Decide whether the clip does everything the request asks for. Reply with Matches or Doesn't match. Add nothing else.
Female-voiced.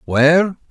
Doesn't match